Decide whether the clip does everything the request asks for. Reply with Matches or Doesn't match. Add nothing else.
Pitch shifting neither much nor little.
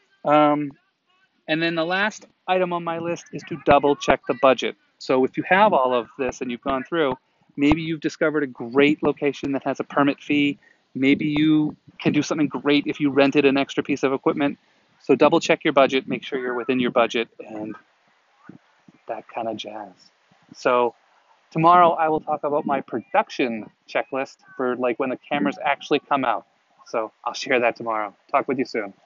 Matches